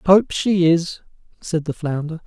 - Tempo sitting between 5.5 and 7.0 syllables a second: No, 4.0 syllables/s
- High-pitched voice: No, medium, 170 Hz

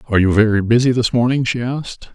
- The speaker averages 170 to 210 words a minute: No, fast, 225 wpm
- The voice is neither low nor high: No, low, 120 Hz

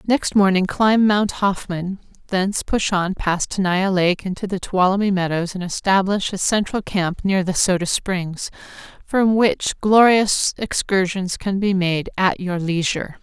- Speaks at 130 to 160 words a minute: Yes, average, 155 wpm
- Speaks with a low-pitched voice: No, high, 190 Hz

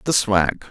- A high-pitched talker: No, low, 105 Hz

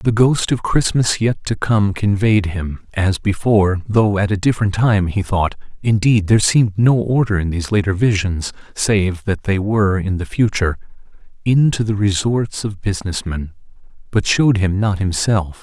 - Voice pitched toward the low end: Yes, low, 100 Hz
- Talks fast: No, average, 165 wpm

